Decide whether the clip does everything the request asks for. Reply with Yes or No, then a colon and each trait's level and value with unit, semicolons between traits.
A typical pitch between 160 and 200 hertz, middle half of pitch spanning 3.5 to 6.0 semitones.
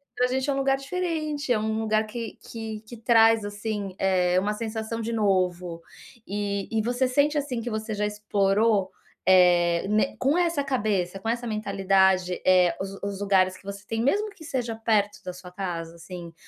No: high, 210 Hz; average, 3.8 semitones